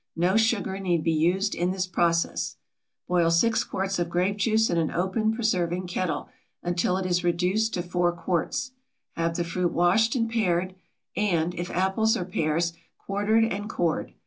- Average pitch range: Yes, average, 3.0 semitones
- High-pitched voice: No, medium, 180 Hz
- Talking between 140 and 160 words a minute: No, average, 170 wpm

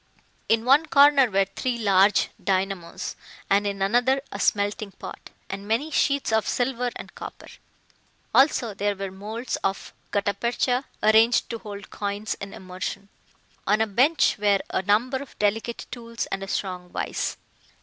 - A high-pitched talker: Yes, high, 210 Hz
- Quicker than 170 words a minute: No, average, 155 wpm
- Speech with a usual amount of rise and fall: Yes, average, 3.6 semitones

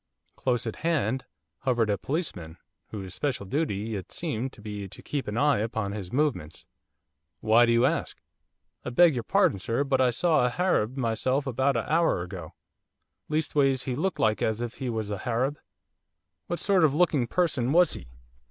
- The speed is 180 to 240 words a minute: Yes, average, 185 wpm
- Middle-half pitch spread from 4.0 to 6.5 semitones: Yes, average, 5.2 semitones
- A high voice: No, low, 125 Hz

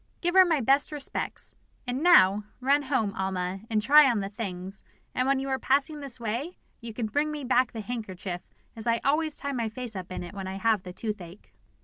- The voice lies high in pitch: Yes, high, 235 Hz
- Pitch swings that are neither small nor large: No, wide, 5.7 semitones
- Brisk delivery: Yes, fast, 220 wpm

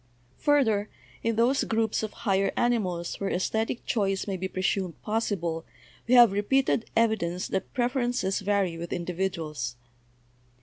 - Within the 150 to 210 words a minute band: No, slow, 135 wpm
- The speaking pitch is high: Yes, high, 200 Hz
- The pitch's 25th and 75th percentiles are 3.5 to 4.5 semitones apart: Yes, average, 4.0 semitones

